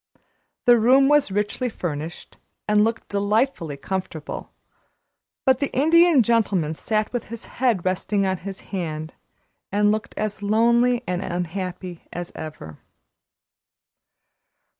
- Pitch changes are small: No, average, 4.9 semitones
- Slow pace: Yes, slow, 120 wpm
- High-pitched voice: Yes, high, 205 Hz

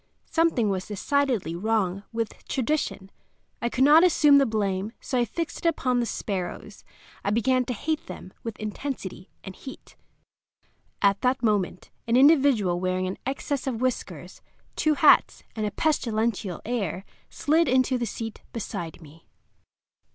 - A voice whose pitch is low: No, high, 230 Hz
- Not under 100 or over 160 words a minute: Yes, average, 150 wpm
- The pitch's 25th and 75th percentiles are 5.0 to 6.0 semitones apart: Yes, wide, 5.5 semitones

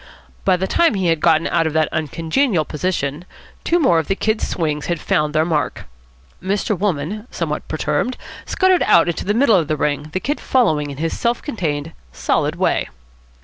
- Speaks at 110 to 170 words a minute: No, average, 190 wpm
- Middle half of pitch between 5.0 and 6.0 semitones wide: Yes, average, 5.3 semitones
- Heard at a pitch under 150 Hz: No, medium, 165 Hz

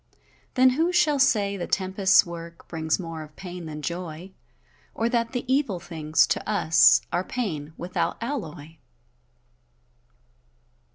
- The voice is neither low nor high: Yes, medium, 180 Hz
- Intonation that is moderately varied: No, wide, 6.2 semitones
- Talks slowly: Yes, slow, 130 wpm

